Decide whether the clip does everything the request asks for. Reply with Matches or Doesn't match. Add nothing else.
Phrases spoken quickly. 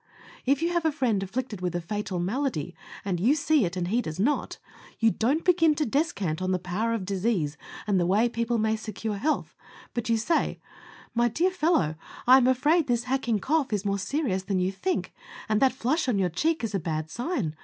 Matches